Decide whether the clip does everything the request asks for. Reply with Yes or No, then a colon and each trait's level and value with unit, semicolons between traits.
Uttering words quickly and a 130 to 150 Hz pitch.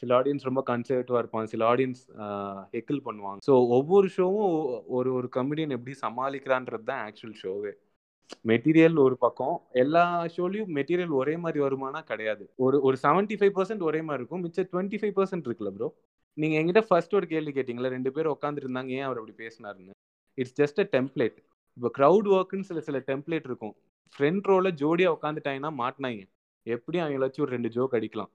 Yes: fast, 165 wpm; low, 135 Hz